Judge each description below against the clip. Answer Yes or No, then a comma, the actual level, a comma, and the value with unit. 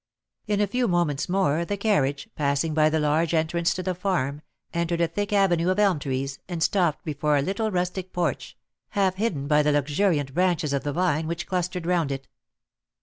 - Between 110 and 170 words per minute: No, average, 195 wpm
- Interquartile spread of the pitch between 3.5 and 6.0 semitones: Yes, average, 4.0 semitones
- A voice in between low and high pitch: Yes, medium, 170 Hz